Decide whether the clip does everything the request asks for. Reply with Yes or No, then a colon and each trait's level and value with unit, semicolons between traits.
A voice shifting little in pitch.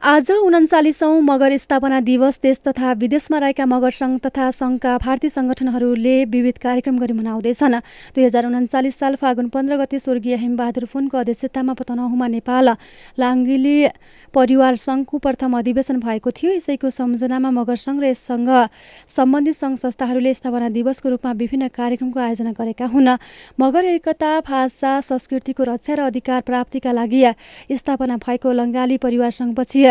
Yes: narrow, 1.6 semitones